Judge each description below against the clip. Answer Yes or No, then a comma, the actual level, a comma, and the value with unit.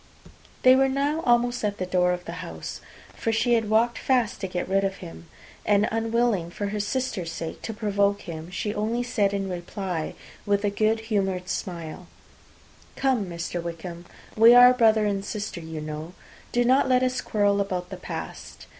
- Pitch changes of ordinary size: Yes, average, 4.5 semitones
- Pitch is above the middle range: Yes, high, 205 Hz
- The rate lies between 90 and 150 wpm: No, average, 180 wpm